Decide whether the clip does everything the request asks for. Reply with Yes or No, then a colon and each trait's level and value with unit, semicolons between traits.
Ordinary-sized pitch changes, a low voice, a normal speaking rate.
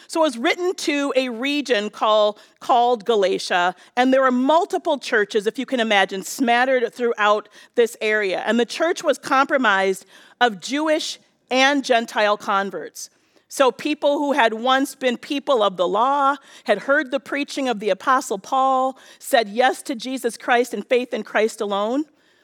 No: average, 4.6 semitones; very high, 255 Hz; average, 165 wpm